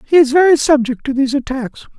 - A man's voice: Yes, male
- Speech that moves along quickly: Yes, fast, 210 wpm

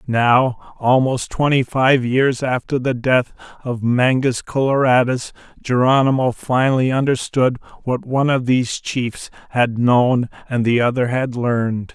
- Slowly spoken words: Yes, slow, 130 wpm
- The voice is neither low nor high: No, low, 125 Hz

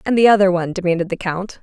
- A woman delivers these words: Yes, female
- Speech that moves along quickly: Yes, fast, 260 wpm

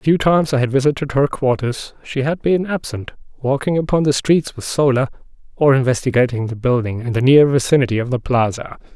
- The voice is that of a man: Yes, male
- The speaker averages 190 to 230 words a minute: Yes, average, 195 wpm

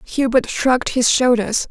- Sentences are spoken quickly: No, average, 140 wpm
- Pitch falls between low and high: No, high, 245 Hz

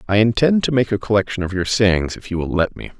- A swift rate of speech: Yes, fast, 280 wpm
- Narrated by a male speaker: Yes, male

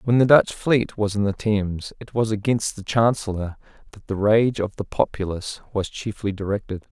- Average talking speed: Yes, average, 190 wpm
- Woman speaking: No, male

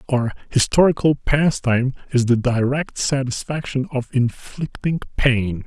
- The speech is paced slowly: Yes, slow, 105 wpm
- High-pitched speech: No, low, 130 Hz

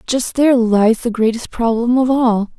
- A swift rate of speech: No, average, 185 wpm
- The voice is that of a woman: Yes, female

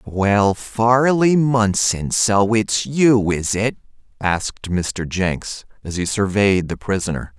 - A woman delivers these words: No, male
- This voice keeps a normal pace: No, slow, 130 wpm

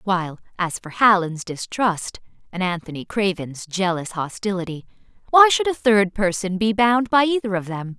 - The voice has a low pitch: No, high, 200 Hz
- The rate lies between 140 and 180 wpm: Yes, average, 160 wpm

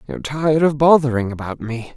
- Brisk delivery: No, average, 185 wpm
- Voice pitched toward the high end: No, low, 135 Hz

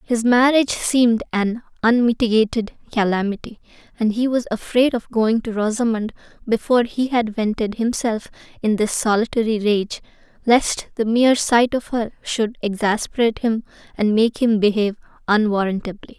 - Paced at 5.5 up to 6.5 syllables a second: No, 5.1 syllables/s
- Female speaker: Yes, female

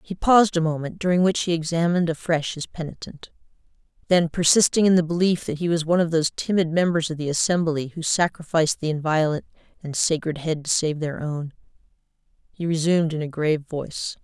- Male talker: No, female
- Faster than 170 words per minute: Yes, average, 185 wpm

